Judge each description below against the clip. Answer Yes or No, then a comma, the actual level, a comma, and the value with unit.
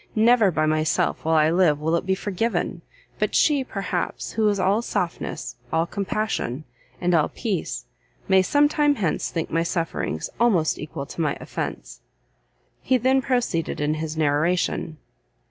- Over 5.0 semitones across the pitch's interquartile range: Yes, wide, 5.6 semitones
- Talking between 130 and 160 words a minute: Yes, average, 155 wpm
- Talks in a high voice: No, medium, 180 Hz